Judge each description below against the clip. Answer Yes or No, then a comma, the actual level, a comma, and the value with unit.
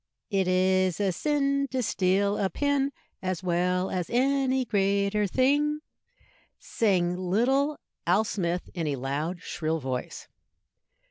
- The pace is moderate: No, slow, 125 wpm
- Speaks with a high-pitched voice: Yes, high, 195 Hz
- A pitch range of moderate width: No, wide, 6.5 semitones